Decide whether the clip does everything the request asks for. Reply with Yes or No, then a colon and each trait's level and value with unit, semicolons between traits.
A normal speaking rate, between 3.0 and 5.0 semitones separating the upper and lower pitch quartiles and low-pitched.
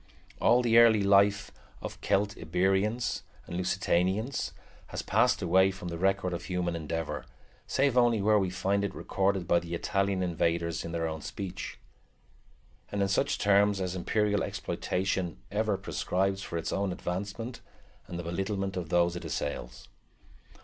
No: average, 150 wpm; narrow, 2.6 semitones; very low, 95 Hz